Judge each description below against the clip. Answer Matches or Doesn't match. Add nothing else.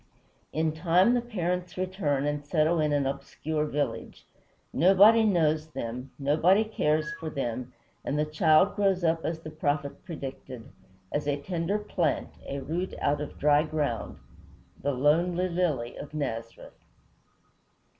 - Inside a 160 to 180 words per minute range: Doesn't match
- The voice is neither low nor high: Matches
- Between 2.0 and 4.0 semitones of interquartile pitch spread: Matches